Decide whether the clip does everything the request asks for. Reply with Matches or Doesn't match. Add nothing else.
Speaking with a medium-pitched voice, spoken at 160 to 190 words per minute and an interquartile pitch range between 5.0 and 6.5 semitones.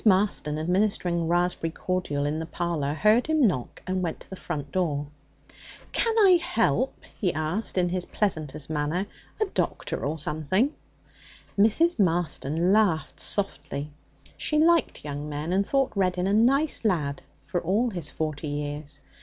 Doesn't match